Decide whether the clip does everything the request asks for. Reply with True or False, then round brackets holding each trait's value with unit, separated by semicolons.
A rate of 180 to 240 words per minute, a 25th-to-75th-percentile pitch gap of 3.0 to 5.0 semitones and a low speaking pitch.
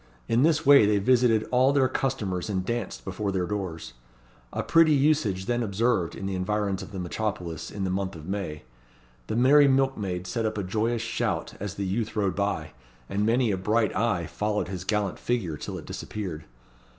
True (190 wpm; 4.1 semitones; 105 Hz)